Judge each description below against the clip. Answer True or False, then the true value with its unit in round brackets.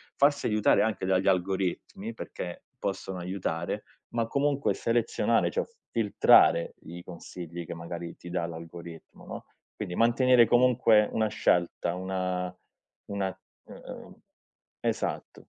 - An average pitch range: True (5.0 semitones)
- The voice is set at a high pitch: False (95 Hz)